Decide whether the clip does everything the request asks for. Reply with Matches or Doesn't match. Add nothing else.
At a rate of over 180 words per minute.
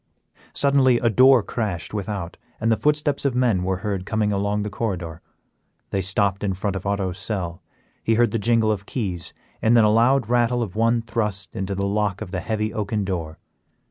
Matches